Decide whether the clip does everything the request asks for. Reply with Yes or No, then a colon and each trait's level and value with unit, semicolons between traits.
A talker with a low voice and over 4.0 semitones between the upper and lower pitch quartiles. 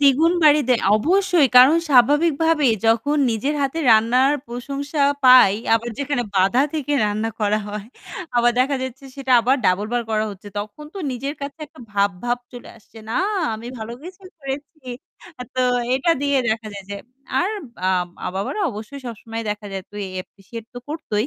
No: very high, 250 Hz; average, 4.8 semitones